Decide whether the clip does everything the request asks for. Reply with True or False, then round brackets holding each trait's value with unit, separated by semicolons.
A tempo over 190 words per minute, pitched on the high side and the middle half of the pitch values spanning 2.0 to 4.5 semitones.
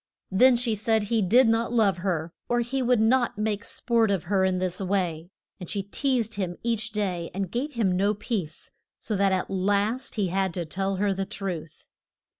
True (200 wpm; 200 Hz; 3.5 semitones)